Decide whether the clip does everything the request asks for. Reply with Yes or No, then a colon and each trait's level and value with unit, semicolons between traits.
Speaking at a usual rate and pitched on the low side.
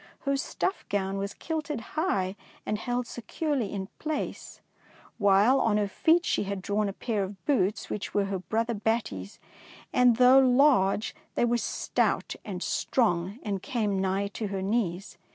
No: average, 165 wpm; high, 210 Hz